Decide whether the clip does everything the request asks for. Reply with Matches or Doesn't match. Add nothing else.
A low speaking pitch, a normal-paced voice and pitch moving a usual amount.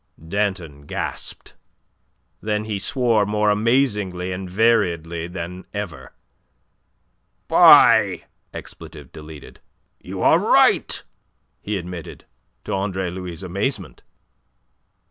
Doesn't match